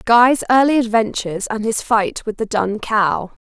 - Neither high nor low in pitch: No, high, 220 Hz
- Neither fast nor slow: Yes, average, 175 wpm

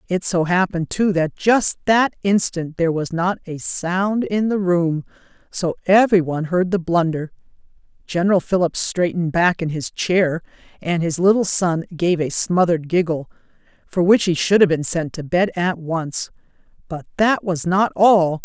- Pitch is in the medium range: Yes, medium, 175 Hz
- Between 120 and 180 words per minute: Yes, average, 165 wpm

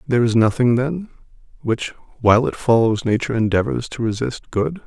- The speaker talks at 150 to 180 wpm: Yes, average, 160 wpm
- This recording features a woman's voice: No, male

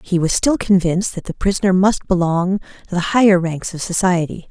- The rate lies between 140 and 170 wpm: No, average, 200 wpm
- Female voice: Yes, female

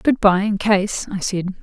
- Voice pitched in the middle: No, high, 200 Hz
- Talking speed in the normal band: No, fast, 220 wpm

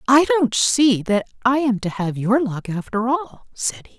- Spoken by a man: No, female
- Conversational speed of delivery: No, fast, 210 wpm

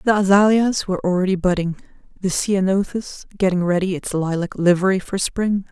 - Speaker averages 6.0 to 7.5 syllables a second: No, 5.4 syllables/s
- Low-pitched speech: No, high, 190 Hz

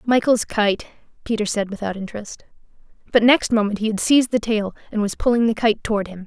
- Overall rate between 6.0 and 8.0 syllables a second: Yes, 6.1 syllables/s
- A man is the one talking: No, female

